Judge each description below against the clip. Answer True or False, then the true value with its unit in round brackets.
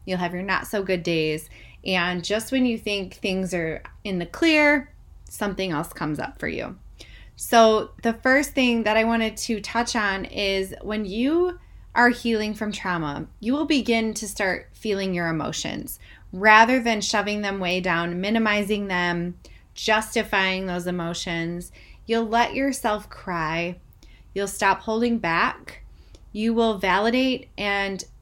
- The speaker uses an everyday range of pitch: True (4.0 semitones)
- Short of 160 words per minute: True (150 wpm)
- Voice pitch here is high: True (210 Hz)